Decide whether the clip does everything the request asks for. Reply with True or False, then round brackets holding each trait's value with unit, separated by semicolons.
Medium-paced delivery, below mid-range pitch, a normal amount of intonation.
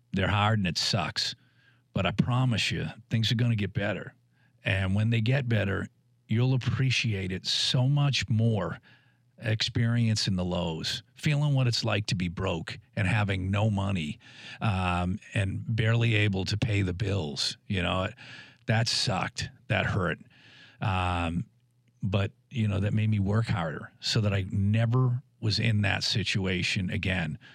True (155 wpm; 110 Hz; 3.8 semitones)